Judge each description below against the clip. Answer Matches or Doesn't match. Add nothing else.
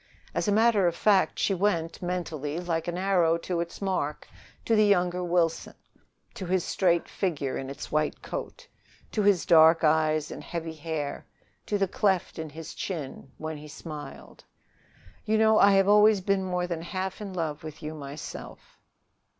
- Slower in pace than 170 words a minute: Doesn't match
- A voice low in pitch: Doesn't match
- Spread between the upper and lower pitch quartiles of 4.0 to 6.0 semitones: Doesn't match